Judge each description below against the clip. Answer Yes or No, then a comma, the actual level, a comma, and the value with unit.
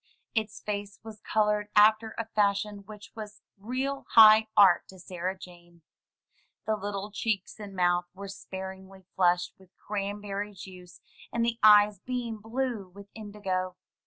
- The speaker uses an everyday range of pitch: No, narrow, 2.3 semitones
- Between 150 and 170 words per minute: No, average, 140 wpm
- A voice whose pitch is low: No, high, 205 Hz